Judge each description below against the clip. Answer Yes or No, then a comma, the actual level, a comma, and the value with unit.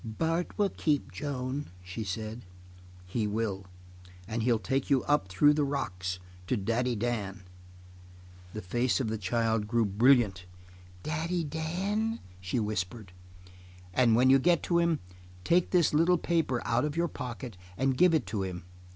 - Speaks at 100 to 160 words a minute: Yes, average, 155 wpm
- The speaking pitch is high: No, low, 125 Hz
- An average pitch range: No, wide, 6.1 semitones